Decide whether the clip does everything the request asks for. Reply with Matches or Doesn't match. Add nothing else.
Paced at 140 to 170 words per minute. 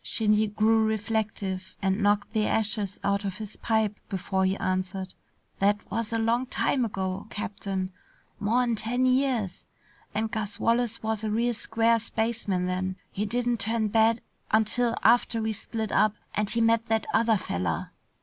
Matches